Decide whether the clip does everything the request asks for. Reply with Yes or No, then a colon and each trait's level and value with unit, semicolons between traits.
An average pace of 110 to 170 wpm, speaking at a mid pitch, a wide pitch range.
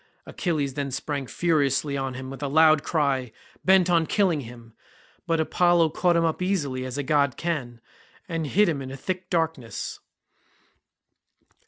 No: average, 160 wpm; medium, 150 Hz; average, 4.0 semitones